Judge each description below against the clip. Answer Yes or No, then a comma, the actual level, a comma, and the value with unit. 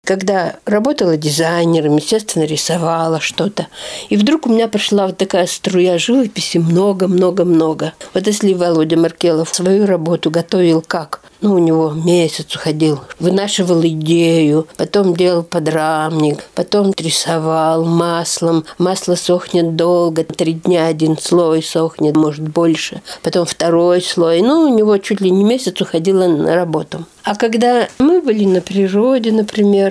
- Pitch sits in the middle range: Yes, medium, 175 Hz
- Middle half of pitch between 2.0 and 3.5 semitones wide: Yes, average, 2.9 semitones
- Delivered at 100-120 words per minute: No, average, 135 wpm